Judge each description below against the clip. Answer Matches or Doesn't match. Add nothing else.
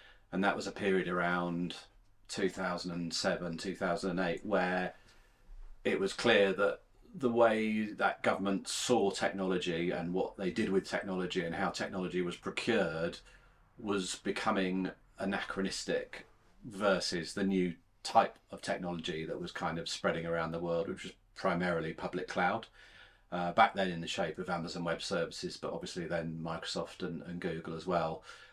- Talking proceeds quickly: Doesn't match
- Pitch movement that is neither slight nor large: Doesn't match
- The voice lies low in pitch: Matches